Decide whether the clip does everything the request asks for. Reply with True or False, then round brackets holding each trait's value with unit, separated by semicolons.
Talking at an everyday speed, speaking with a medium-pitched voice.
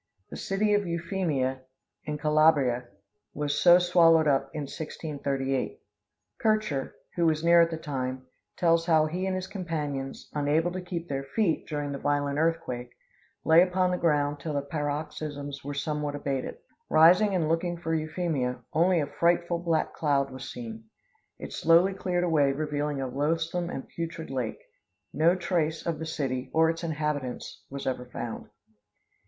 True (160 wpm; 155 Hz)